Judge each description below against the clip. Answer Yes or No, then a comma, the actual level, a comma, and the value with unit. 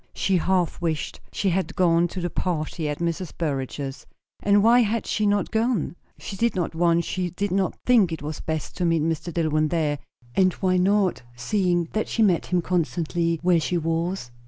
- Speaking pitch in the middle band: Yes, medium, 175 Hz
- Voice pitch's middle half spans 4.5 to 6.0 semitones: No, average, 2.8 semitones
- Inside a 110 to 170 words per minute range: No, average, 190 wpm